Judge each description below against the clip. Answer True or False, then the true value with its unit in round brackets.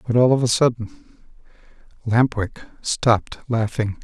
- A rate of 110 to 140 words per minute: True (135 wpm)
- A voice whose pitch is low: True (115 Hz)